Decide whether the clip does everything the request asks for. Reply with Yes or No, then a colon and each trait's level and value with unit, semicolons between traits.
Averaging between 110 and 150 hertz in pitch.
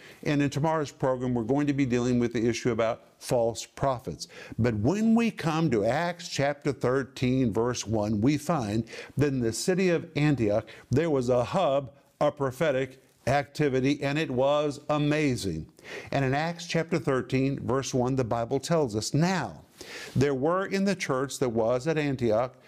Yes: medium, 140 Hz